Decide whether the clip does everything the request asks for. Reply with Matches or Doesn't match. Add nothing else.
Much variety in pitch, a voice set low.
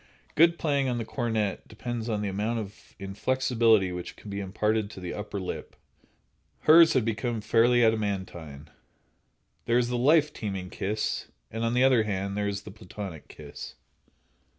Doesn't match